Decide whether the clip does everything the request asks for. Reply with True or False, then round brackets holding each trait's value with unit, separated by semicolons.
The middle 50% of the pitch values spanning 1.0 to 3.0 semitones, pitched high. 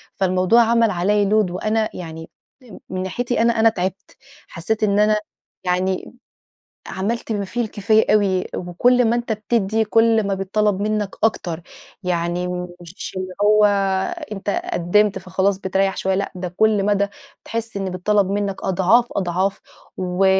True (2.7 semitones; 200 Hz)